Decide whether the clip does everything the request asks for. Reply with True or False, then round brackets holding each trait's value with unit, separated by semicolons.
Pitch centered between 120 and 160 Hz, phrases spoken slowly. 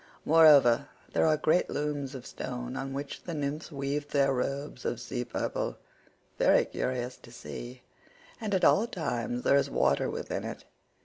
False (140 Hz; 150 wpm)